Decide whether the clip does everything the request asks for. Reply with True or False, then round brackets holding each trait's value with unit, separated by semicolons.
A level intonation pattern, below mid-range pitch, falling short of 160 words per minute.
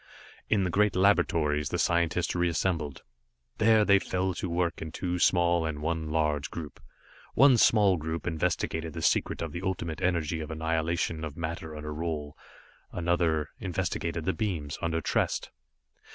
True (2.3 semitones; 85 Hz; 150 wpm)